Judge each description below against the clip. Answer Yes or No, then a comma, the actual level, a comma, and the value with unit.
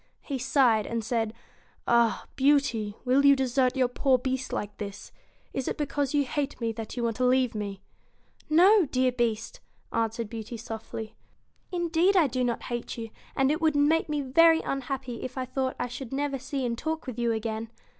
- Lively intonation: No, average, 3.5 semitones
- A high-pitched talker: Yes, very high, 255 Hz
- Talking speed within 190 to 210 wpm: Yes, average, 200 wpm